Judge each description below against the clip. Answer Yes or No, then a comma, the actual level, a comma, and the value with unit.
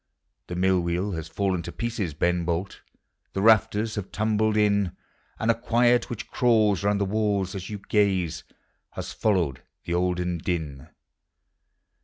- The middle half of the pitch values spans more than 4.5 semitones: No, average, 3.5 semitones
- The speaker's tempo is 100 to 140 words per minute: No, average, 150 wpm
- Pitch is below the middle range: Yes, low, 100 Hz